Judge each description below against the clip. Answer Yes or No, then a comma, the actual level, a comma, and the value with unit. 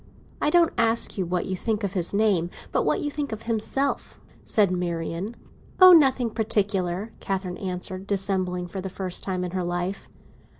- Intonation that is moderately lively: Yes, average, 3.6 semitones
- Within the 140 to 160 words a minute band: No, average, 175 wpm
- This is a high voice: Yes, high, 195 Hz